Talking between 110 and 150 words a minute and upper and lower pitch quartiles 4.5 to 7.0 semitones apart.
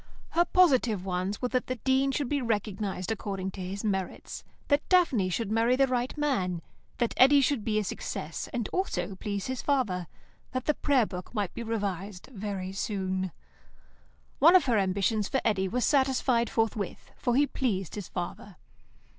No: average, 170 wpm; average, 5.2 semitones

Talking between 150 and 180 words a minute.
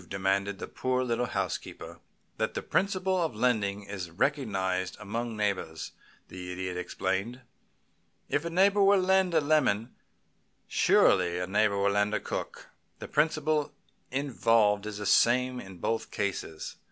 No: average, 140 wpm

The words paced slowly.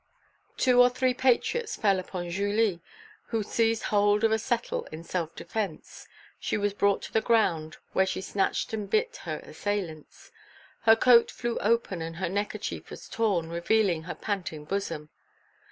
No: average, 160 wpm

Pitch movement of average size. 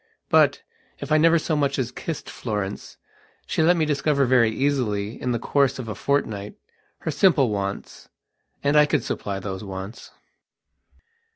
No: wide, 6.0 semitones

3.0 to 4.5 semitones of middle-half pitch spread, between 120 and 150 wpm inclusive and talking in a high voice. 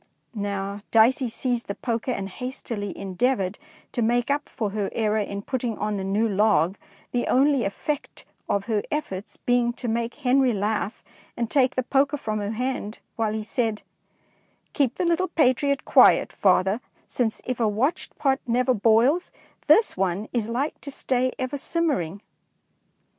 No: average, 3.9 semitones; average, 165 wpm; high, 230 Hz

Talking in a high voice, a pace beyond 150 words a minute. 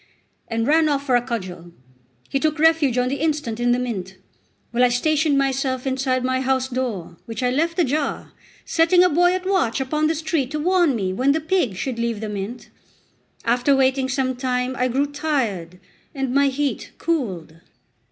Yes: very high, 260 Hz; average, 180 wpm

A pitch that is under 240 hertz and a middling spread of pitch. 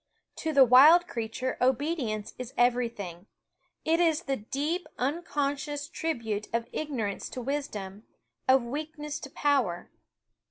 No: very high, 270 Hz; average, 4.5 semitones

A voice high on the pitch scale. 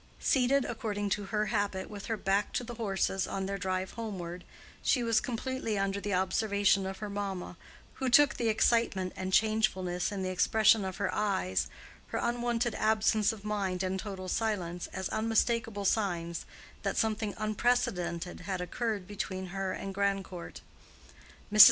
Yes: high, 200 Hz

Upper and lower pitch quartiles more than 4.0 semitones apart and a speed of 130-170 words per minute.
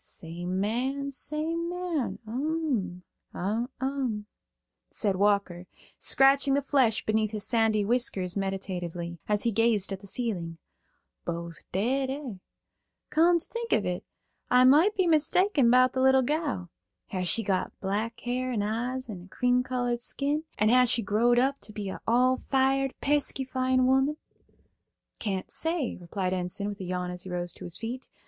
Yes: wide, 5.5 semitones; average, 160 wpm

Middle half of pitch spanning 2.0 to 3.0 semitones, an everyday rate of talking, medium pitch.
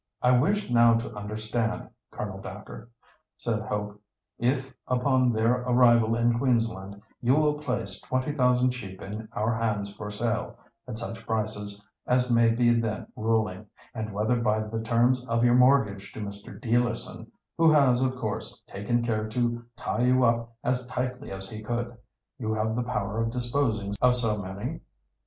No: narrow, 2.5 semitones; average, 150 wpm; low, 115 Hz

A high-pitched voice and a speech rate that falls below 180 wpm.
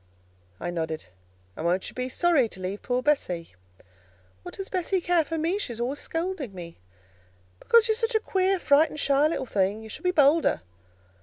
No: very high, 285 Hz; average, 185 wpm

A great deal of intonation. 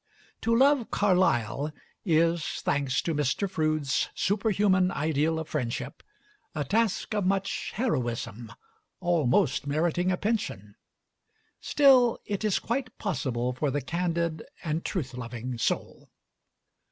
Yes: wide, 6.7 semitones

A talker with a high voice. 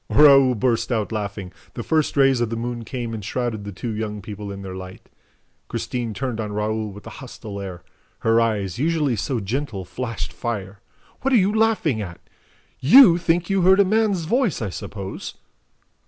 No: low, 115 Hz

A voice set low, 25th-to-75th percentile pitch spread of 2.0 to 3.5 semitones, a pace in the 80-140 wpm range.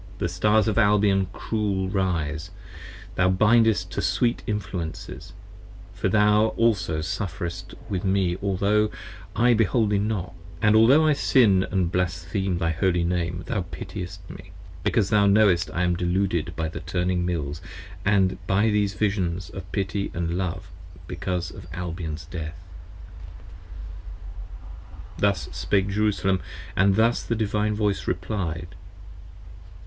Yes: very low, 95 Hz; average, 3.1 semitones; slow, 135 wpm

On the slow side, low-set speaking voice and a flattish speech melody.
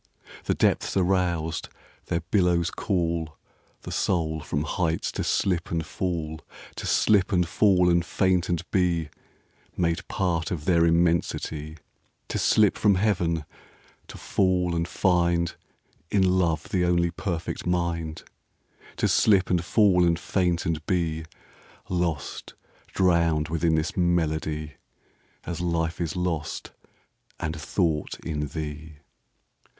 Yes: slow, 110 wpm; very low, 85 Hz; narrow, 2.0 semitones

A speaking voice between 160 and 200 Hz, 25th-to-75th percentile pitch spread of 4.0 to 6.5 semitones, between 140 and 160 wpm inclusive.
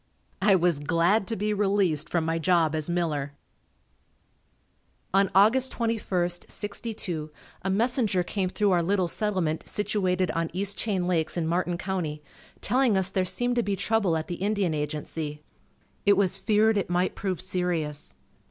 No: medium, 185 Hz; average, 3.5 semitones; average, 155 wpm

